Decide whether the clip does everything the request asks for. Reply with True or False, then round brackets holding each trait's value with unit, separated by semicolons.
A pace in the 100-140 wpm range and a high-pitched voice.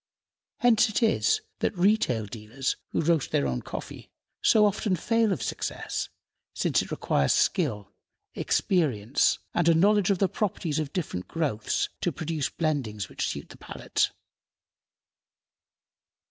False (135 wpm; 165 Hz)